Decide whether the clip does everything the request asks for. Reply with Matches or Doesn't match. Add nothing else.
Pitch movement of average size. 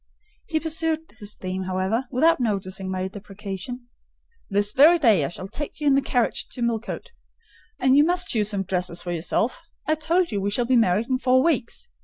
Doesn't match